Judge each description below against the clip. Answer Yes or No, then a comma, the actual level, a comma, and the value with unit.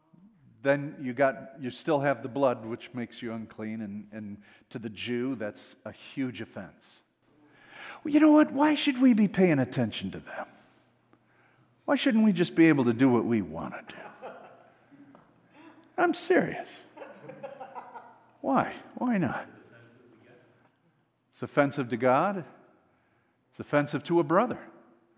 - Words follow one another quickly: No, average, 145 wpm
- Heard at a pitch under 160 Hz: Yes, low, 135 Hz